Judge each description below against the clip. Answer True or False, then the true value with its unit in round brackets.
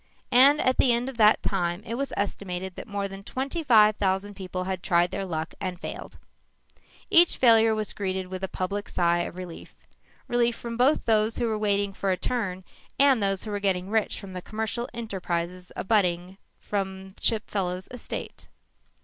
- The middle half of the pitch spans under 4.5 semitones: True (3.5 semitones)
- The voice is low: False (200 Hz)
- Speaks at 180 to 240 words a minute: True (185 wpm)